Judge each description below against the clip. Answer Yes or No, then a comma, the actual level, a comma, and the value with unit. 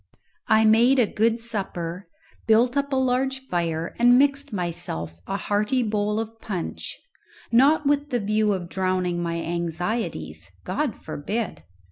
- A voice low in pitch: No, high, 215 Hz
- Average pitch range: No, wide, 5.7 semitones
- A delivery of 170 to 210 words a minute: No, average, 140 wpm